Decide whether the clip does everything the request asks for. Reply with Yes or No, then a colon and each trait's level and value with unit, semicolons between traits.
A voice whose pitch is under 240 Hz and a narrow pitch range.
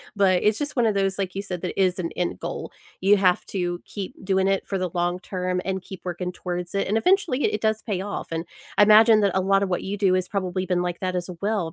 Yes: high, 190 Hz; narrow, 2.0 semitones